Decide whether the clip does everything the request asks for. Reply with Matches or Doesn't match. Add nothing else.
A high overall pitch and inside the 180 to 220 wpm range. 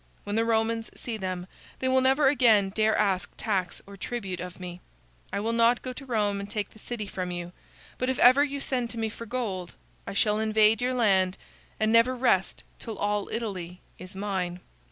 Matches